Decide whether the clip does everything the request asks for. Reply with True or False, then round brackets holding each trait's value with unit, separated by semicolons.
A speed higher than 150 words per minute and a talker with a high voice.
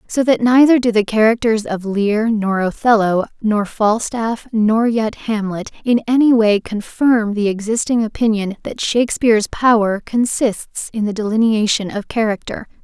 False (145 wpm; 220 Hz)